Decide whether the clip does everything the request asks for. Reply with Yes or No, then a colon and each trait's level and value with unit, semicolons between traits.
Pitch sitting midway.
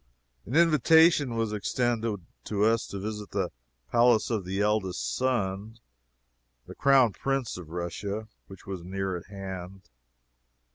No: low, 105 Hz